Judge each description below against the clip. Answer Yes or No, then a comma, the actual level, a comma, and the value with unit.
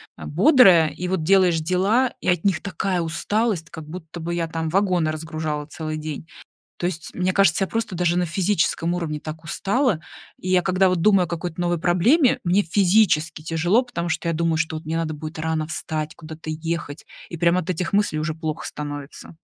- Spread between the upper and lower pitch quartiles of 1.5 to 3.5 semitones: Yes, average, 2.7 semitones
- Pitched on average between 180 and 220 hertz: No, medium, 170 Hz